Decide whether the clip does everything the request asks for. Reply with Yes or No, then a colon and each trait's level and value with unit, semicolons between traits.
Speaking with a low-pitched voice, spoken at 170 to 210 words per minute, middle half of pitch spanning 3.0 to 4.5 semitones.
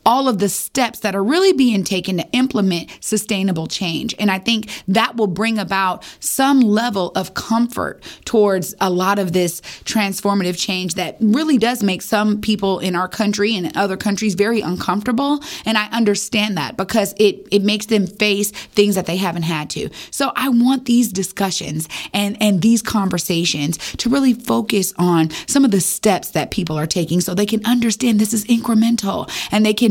No: high, 205 Hz; average, 185 wpm; average, 3.4 semitones